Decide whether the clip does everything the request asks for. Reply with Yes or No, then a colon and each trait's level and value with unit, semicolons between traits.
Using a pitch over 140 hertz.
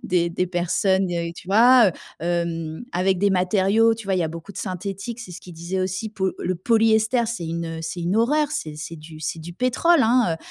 Yes: medium, 185 Hz